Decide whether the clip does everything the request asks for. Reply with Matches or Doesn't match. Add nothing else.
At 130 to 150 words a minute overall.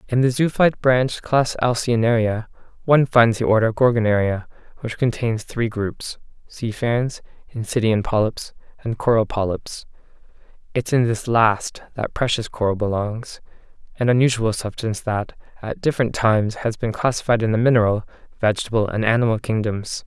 Matches